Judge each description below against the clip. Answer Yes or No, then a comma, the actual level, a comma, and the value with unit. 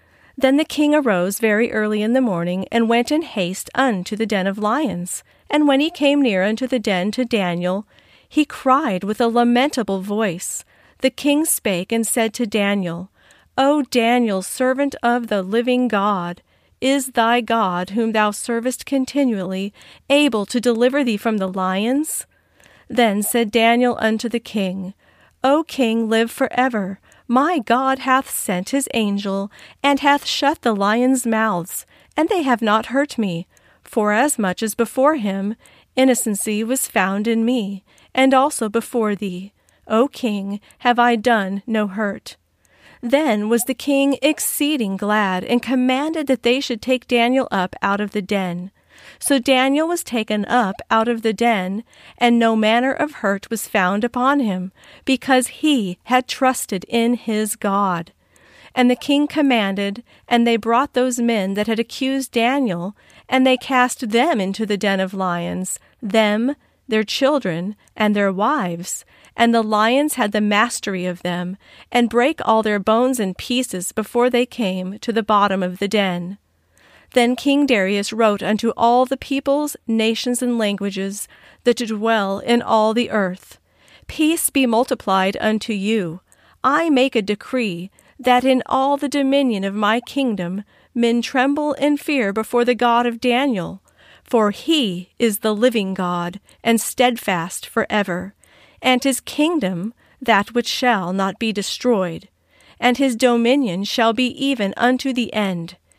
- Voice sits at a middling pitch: No, high, 230 Hz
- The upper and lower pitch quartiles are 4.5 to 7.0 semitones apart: No, average, 4.1 semitones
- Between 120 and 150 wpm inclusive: No, average, 160 wpm